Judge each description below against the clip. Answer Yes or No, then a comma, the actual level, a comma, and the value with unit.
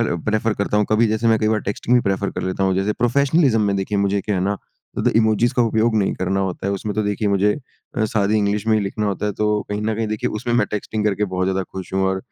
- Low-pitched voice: Yes, low, 105 Hz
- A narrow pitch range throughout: Yes, narrow, 1.9 semitones